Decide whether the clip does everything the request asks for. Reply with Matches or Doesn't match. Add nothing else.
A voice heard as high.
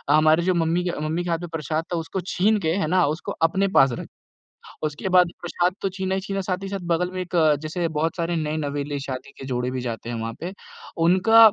Doesn't match